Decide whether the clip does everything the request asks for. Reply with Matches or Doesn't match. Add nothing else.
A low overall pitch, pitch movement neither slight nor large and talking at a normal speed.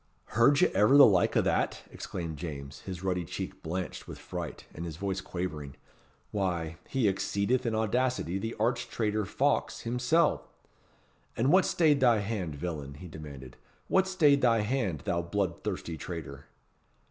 Doesn't match